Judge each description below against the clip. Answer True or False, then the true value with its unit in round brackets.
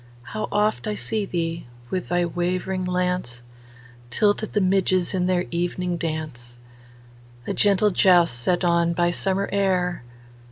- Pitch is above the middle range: False (175 Hz)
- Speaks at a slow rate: True (130 wpm)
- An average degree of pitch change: False (7.2 semitones)